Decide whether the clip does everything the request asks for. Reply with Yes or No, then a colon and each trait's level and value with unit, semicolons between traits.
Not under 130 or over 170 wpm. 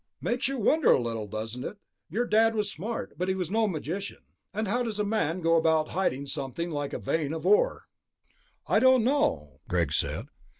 No: average, 200 wpm